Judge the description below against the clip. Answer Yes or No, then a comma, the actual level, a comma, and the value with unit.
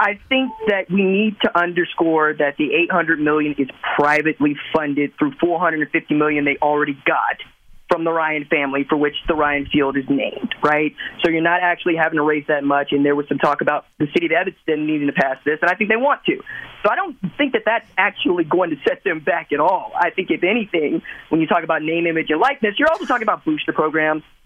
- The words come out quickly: Yes, fast, 240 wpm